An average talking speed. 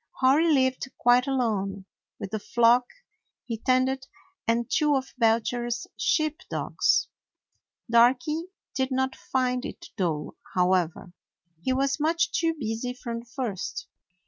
No: slow, 125 wpm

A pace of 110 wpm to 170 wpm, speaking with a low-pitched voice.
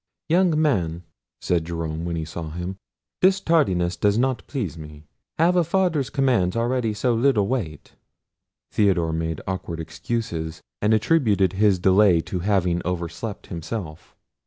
Yes: average, 140 wpm; very low, 95 Hz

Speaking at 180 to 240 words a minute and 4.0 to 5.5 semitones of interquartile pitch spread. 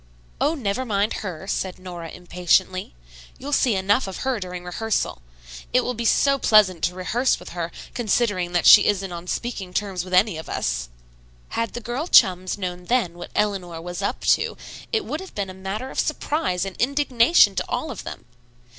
Yes: average, 190 wpm; average, 5.0 semitones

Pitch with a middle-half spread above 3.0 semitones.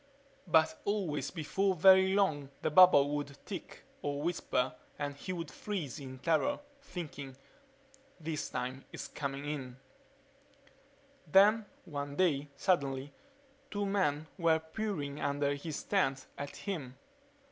Yes: average, 4.6 semitones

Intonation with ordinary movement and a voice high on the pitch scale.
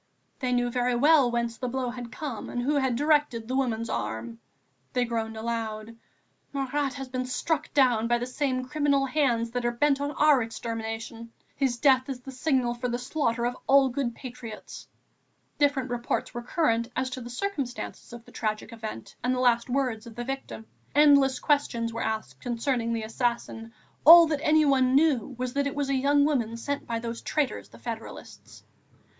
Yes: average, 3.0 semitones; very high, 250 Hz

